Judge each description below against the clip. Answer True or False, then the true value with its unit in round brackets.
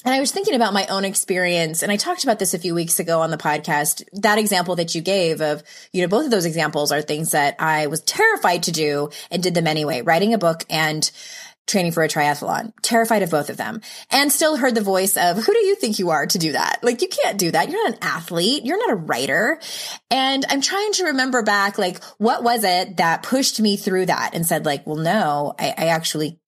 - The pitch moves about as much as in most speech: False (6.3 semitones)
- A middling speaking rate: False (245 wpm)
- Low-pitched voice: False (185 Hz)